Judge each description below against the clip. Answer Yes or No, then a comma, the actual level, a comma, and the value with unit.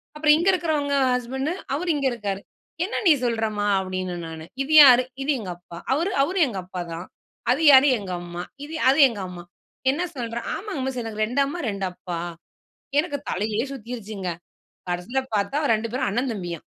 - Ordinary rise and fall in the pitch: No, wide, 6.6 semitones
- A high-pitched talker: Yes, high, 235 Hz